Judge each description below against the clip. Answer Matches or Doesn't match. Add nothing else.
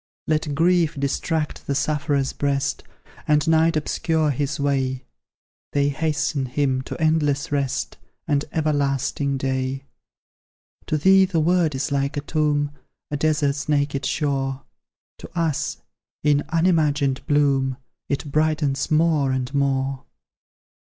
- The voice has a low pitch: Doesn't match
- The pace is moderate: Doesn't match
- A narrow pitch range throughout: Matches